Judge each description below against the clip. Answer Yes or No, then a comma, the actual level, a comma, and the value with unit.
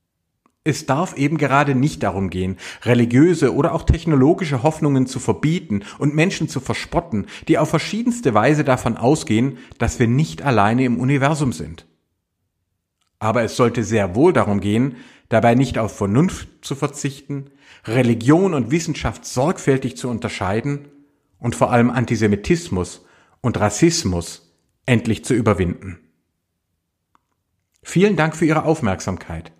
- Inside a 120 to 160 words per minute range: Yes, average, 130 wpm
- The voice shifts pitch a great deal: Yes, wide, 6.2 semitones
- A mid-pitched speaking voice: No, low, 120 Hz